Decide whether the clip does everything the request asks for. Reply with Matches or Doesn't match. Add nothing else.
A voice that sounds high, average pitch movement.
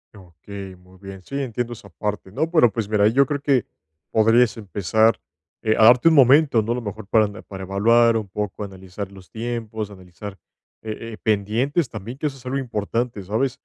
Doesn't match